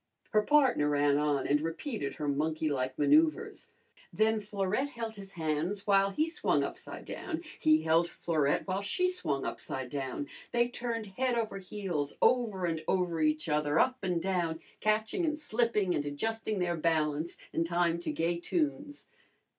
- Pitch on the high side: No, medium, 180 Hz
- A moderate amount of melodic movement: No, wide, 6.4 semitones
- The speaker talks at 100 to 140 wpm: No, average, 160 wpm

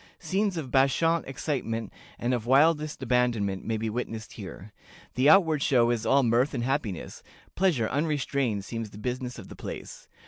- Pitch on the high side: No, low, 125 Hz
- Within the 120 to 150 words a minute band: No, average, 165 wpm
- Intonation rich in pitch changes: No, average, 4.3 semitones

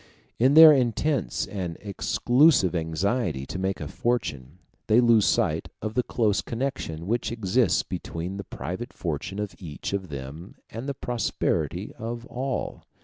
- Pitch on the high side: No, low, 105 Hz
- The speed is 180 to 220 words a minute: No, average, 145 wpm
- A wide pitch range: Yes, wide, 5.8 semitones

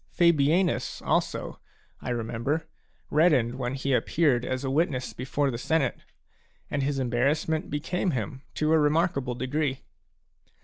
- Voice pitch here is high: No, medium, 140 Hz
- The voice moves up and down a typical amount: Yes, average, 3.6 semitones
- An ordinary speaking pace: No, slow, 130 wpm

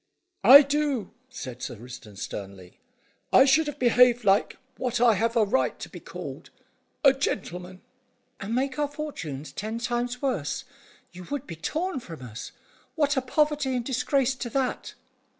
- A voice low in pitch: No, high, 245 Hz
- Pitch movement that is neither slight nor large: No, wide, 7.2 semitones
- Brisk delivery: No, average, 160 wpm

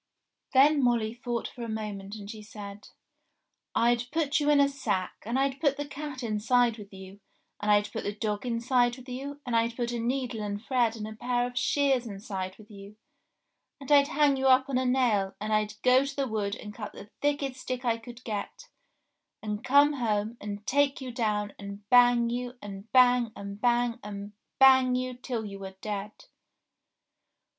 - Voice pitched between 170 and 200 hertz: No, high, 235 Hz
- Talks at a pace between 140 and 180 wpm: No, average, 195 wpm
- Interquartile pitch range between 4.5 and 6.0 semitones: No, average, 3.7 semitones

